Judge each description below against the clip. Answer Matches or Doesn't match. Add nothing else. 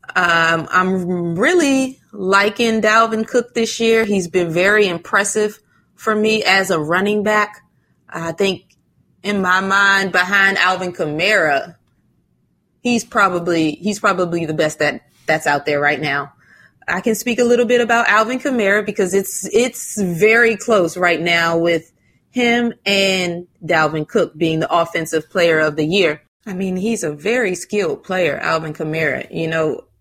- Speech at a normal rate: Matches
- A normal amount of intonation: Matches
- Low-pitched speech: Doesn't match